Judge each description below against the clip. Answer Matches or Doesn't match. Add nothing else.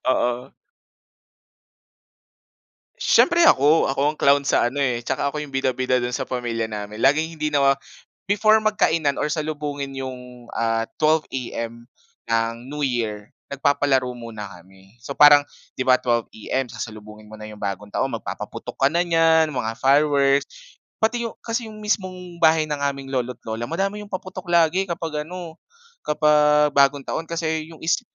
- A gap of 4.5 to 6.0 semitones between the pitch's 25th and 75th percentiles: Matches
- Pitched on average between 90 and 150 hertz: Matches